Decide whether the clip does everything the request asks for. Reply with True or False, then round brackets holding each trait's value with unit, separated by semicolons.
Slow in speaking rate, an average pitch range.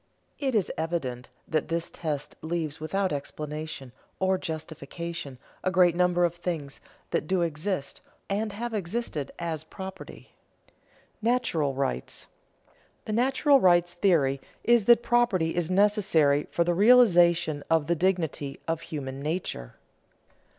True (130 wpm; 4.1 semitones)